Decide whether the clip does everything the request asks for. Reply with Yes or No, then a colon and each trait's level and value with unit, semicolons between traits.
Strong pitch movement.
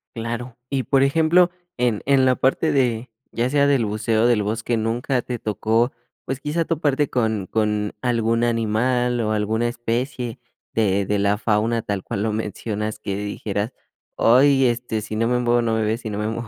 No: average, 2.7 semitones